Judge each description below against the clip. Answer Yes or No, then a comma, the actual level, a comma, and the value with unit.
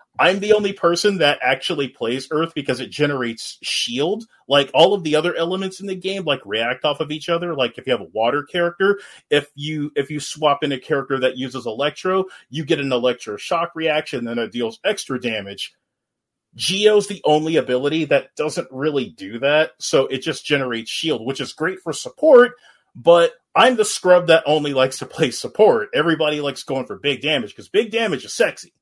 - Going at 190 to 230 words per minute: Yes, average, 200 wpm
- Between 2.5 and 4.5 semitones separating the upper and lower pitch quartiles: No, average, 4.9 semitones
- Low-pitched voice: No, medium, 150 Hz